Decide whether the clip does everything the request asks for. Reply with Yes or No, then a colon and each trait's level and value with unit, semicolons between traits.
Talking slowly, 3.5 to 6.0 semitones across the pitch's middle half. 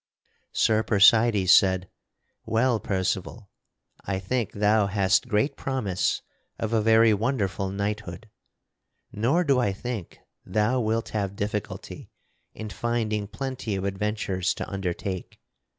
No: slow, 120 wpm; average, 2.8 semitones